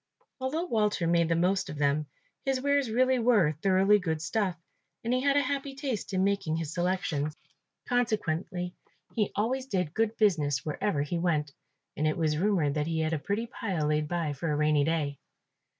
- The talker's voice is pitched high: No, medium, 180 Hz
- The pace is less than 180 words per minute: No, average, 185 wpm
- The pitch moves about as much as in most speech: No, wide, 6.5 semitones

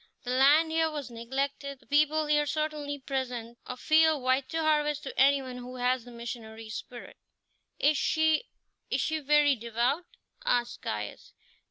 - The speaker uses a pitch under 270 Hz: No, very high, 275 Hz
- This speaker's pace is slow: No, average, 155 wpm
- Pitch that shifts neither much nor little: Yes, average, 3.5 semitones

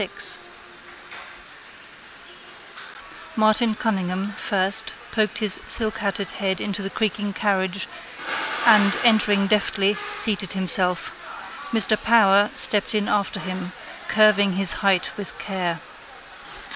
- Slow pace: Yes, slow, 105 wpm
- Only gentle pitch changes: Yes, narrow, 2.1 semitones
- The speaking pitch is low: No, high, 200 Hz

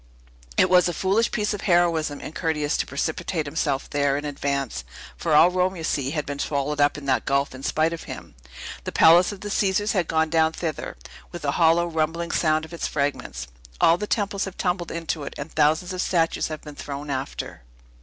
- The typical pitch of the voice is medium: Yes, medium, 160 Hz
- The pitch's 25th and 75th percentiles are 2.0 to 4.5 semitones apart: Yes, average, 3.3 semitones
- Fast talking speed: Yes, fast, 210 wpm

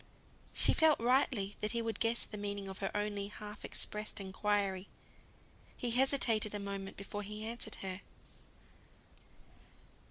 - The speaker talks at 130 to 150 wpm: Yes, slow, 135 wpm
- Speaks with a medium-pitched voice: No, high, 210 Hz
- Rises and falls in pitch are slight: Yes, narrow, 2.3 semitones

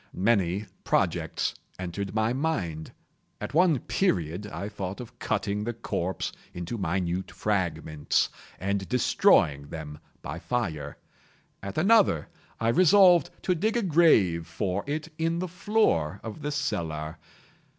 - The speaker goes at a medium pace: No, slow, 130 wpm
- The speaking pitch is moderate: No, low, 100 Hz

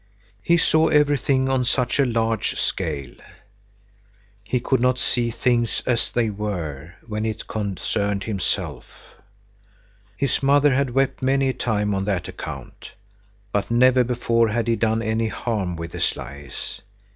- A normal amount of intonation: Yes, average, 3.9 semitones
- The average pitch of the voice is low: Yes, low, 115 Hz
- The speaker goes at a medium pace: Yes, average, 145 wpm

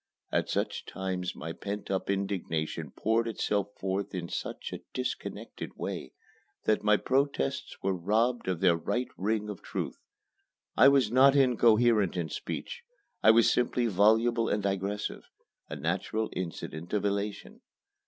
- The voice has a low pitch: Yes, low, 105 Hz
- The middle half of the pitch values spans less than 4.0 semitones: Yes, average, 3.6 semitones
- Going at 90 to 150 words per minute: Yes, average, 145 wpm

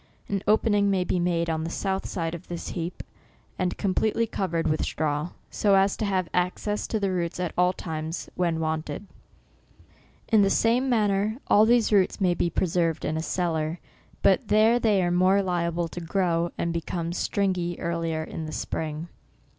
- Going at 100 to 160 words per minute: No, average, 180 wpm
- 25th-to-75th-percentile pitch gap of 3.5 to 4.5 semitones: No, average, 3.0 semitones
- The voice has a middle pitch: Yes, medium, 180 Hz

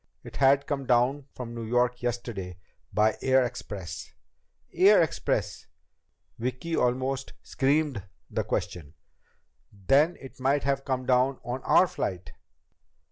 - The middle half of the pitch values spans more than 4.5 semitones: No, average, 2.8 semitones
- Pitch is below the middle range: Yes, low, 125 Hz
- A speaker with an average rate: No, slow, 130 wpm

